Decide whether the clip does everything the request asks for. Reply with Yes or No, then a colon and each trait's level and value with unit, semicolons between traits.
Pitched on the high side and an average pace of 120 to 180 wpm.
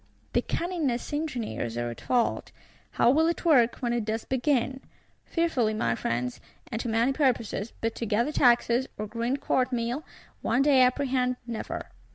Yes: high, 245 Hz; average, 165 wpm